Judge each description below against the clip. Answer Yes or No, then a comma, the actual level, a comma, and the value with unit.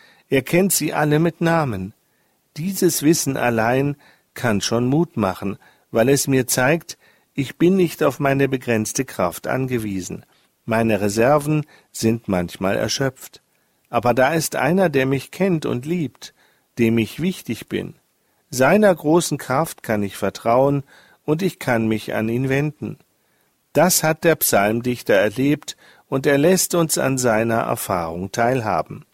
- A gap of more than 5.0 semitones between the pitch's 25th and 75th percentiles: Yes, wide, 5.6 semitones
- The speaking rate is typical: Yes, average, 140 wpm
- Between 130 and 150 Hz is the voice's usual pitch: Yes, low, 135 Hz